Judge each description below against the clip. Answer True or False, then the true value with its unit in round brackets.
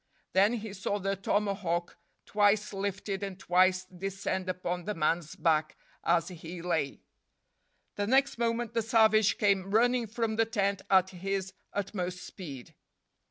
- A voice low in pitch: False (195 Hz)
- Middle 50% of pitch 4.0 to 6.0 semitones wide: False (2.7 semitones)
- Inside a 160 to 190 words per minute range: False (140 wpm)